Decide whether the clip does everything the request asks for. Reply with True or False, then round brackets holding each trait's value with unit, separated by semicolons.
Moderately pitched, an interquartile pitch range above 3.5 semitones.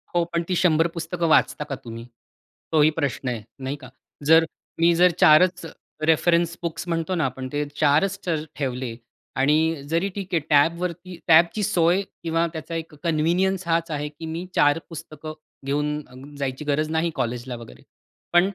False (160 Hz; 2.8 semitones)